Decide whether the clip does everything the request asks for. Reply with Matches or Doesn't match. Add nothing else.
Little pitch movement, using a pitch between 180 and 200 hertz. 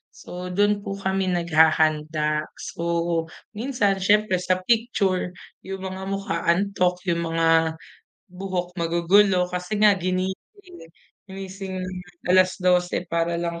Matches